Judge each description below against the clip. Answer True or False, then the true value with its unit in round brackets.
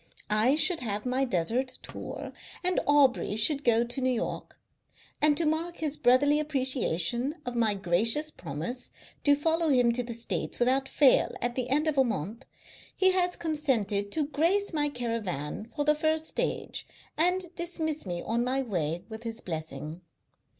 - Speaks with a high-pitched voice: True (255 Hz)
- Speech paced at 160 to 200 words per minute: True (165 wpm)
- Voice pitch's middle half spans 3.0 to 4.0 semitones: False (5.3 semitones)